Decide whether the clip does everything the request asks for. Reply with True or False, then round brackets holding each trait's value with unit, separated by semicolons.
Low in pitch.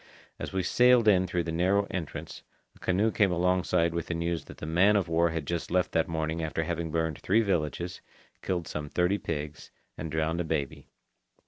True (85 Hz)